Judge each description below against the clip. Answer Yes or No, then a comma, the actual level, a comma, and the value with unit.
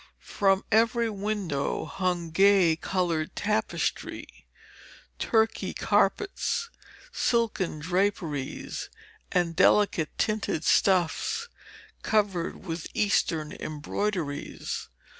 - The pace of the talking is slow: Yes, slow, 75 wpm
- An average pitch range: Yes, average, 4.5 semitones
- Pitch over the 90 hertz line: Yes, high, 190 Hz